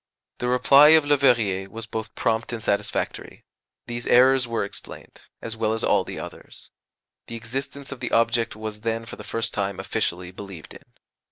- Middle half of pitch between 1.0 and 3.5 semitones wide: Yes, average, 2.7 semitones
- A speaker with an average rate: Yes, average, 175 wpm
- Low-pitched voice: Yes, low, 115 Hz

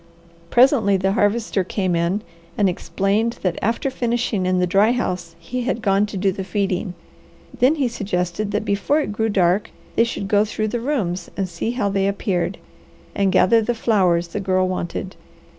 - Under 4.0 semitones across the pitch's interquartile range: Yes, average, 3.5 semitones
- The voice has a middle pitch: No, high, 200 Hz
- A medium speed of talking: Yes, average, 180 wpm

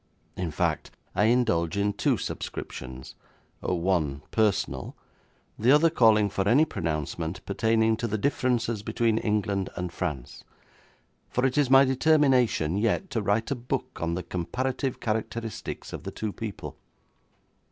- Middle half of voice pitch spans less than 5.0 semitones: No, wide, 5.5 semitones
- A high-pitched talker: No, low, 110 Hz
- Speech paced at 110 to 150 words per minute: Yes, average, 140 wpm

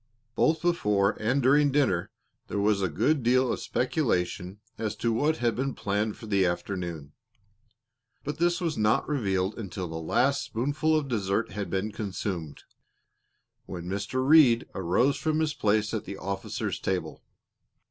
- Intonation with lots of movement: Yes, wide, 6.3 semitones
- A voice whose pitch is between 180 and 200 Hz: No, low, 110 Hz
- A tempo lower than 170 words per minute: Yes, average, 155 wpm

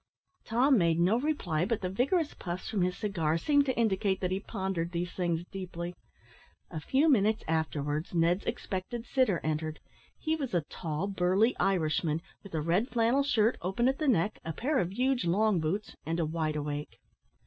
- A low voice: No, high, 190 Hz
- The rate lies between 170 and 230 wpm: Yes, average, 180 wpm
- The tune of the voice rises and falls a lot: Yes, wide, 5.8 semitones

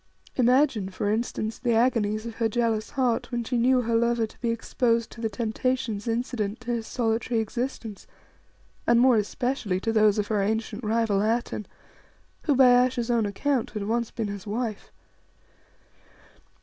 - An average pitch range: No, narrow, 2.2 semitones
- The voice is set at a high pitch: Yes, high, 230 Hz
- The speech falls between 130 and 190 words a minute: Yes, average, 160 wpm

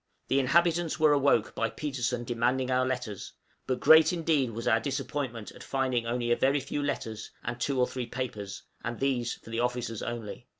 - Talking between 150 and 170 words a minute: No, average, 185 wpm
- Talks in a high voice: No, low, 125 Hz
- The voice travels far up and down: No, average, 2.8 semitones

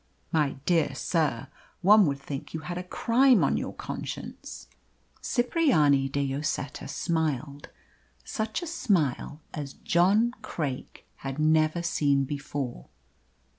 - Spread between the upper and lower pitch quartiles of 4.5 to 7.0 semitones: Yes, average, 4.8 semitones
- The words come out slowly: Yes, slow, 120 wpm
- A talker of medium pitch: Yes, medium, 155 Hz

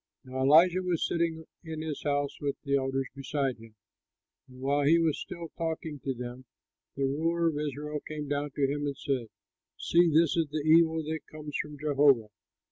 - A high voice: No, medium, 150 Hz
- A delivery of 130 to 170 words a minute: No, average, 185 wpm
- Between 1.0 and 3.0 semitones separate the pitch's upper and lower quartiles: Yes, narrow, 2.6 semitones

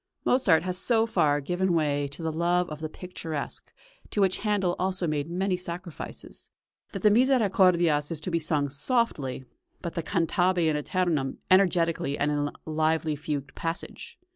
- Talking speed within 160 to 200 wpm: Yes, average, 165 wpm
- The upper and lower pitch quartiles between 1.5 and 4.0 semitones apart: Yes, average, 3.6 semitones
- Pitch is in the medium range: Yes, medium, 170 Hz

